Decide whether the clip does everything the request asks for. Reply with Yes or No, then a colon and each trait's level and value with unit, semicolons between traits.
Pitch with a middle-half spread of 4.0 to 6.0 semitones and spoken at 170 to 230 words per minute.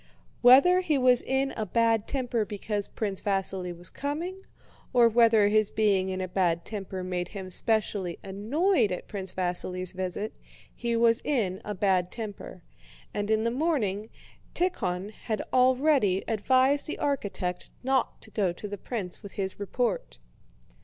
No: average, 4.8 semitones; average, 155 wpm